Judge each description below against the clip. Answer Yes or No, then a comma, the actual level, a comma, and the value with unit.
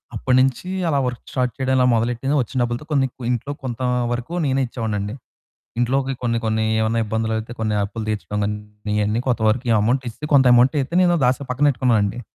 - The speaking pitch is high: No, low, 120 Hz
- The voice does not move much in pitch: No, average, 3.0 semitones